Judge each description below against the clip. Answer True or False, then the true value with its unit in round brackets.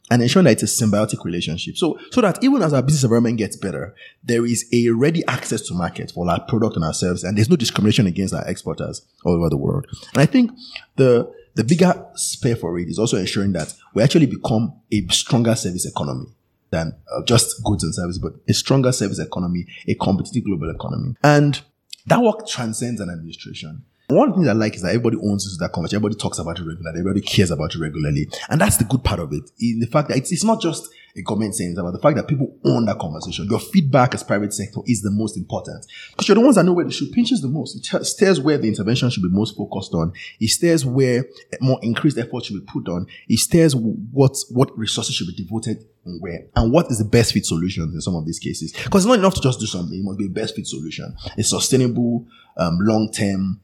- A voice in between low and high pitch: False (110 Hz)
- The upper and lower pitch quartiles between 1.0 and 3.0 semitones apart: False (5.4 semitones)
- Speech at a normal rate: False (240 wpm)